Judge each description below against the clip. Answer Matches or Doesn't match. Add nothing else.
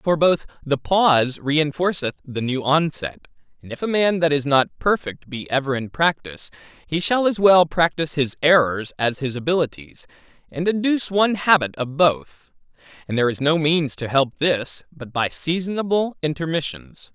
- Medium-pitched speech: Matches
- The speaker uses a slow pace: Doesn't match